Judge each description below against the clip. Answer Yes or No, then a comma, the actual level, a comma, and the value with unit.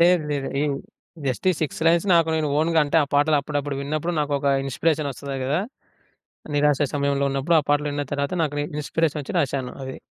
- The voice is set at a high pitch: No, medium, 145 Hz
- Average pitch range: No, narrow, 2.0 semitones